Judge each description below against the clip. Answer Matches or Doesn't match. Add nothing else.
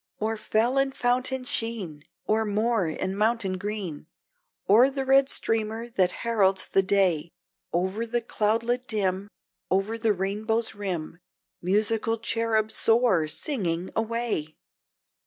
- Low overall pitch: Doesn't match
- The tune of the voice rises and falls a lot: Doesn't match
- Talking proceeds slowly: Matches